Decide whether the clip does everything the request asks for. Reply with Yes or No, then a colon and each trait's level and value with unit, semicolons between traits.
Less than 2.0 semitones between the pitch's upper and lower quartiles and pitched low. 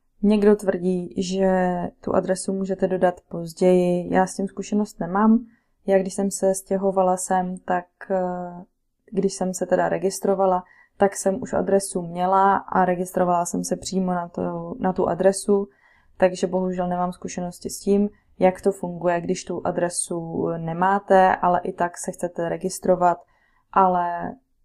No: narrow, 1.5 semitones; medium, 185 Hz